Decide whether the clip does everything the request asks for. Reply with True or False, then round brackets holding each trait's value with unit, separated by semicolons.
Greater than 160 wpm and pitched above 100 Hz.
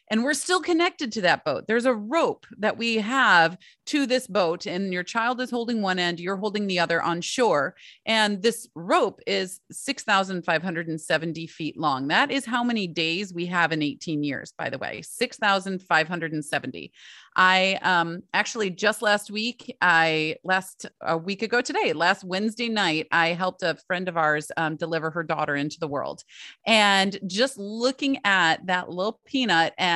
True (170 wpm; 190 Hz)